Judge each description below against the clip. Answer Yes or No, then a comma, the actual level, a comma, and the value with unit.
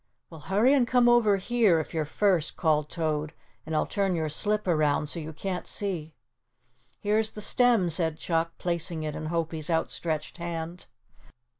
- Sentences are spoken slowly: No, average, 165 wpm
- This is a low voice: No, medium, 170 Hz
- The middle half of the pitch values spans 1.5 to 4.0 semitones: No, average, 4.4 semitones